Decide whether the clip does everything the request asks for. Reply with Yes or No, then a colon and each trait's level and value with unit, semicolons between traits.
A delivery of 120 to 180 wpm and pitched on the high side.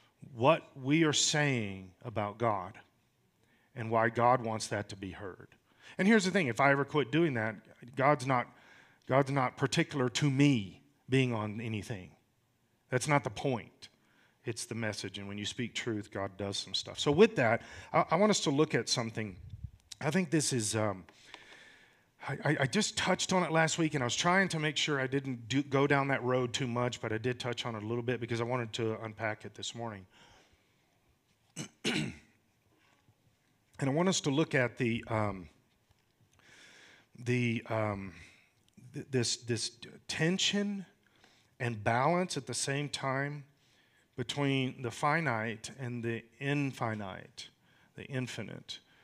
No: average, 165 wpm; low, 125 Hz